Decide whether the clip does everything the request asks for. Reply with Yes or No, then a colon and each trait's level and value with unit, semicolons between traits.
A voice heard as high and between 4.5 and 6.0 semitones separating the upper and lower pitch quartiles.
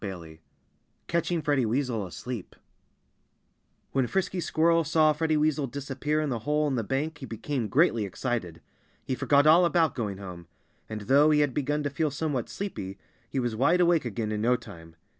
No: low, 135 Hz; wide, 5.6 semitones